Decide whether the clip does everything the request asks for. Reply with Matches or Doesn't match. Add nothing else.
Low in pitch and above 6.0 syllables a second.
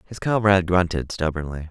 Doesn't match